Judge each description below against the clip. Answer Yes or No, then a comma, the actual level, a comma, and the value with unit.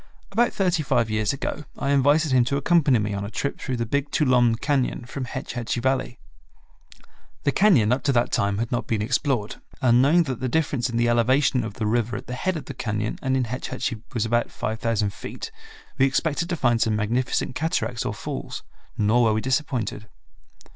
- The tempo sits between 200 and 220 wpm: Yes, fast, 205 wpm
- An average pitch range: Yes, average, 3.7 semitones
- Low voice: Yes, low, 125 Hz